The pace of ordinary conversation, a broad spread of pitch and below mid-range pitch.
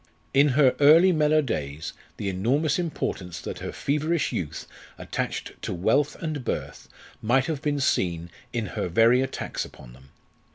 Yes: average, 155 wpm; wide, 8.5 semitones; low, 130 Hz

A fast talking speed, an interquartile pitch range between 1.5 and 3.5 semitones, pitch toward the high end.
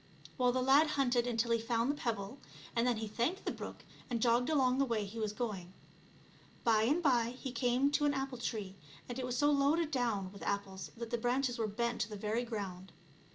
Yes: fast, 220 wpm; average, 3.2 semitones; high, 240 Hz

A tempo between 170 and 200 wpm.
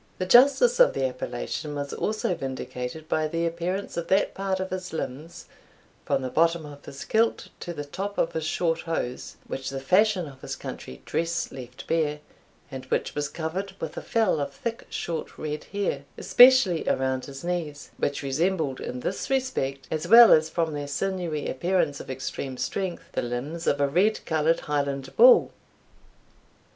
Yes: average, 175 wpm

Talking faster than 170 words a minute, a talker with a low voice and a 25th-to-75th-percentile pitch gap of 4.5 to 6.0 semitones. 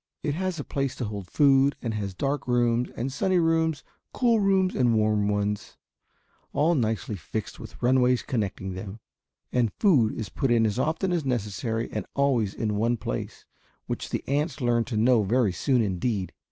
Yes: average, 180 wpm; low, 120 Hz; average, 4.9 semitones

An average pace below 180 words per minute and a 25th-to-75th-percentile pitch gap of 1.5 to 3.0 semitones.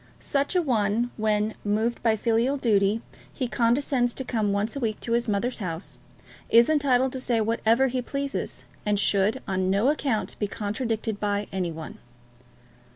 No: average, 165 wpm; average, 3.5 semitones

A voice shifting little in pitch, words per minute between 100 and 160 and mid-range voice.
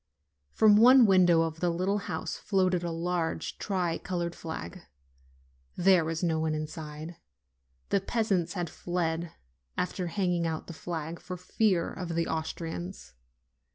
Yes: narrow, 2.2 semitones; average, 145 wpm; medium, 175 Hz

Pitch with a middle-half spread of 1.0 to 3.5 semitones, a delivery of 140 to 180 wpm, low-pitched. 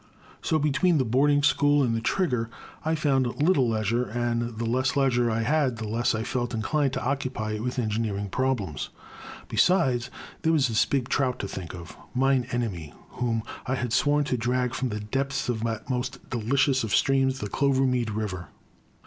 No: average, 3.2 semitones; average, 190 wpm; low, 125 Hz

